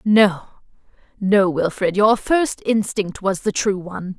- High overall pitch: Yes, high, 200 Hz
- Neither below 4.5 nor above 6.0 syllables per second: No, 3.9 syllables/s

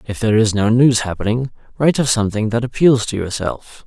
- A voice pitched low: Yes, low, 115 Hz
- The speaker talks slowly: No, average, 200 wpm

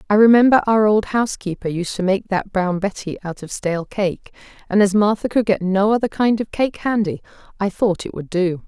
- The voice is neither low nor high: No, high, 200 Hz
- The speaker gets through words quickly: Yes, fast, 215 wpm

